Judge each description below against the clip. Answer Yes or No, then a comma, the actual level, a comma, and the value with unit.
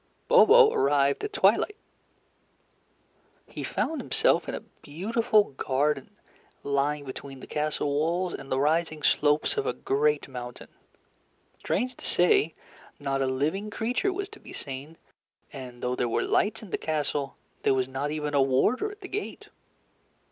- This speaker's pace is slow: No, average, 155 wpm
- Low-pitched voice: No, medium, 150 Hz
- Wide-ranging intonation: Yes, wide, 8.3 semitones